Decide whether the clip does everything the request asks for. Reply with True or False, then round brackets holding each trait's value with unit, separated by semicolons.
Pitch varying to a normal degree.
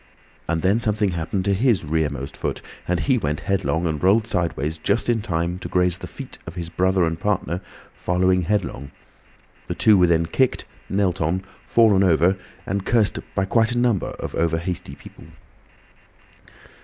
True (3.6 semitones)